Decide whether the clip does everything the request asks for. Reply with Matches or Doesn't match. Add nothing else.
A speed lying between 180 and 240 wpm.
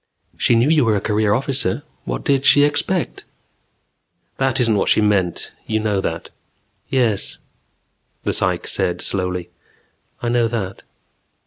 Doesn't match